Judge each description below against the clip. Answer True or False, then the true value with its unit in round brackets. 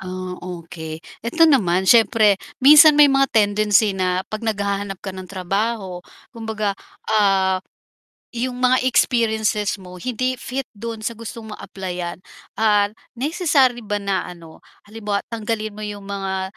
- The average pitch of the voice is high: True (210 Hz)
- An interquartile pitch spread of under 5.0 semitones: True (3.5 semitones)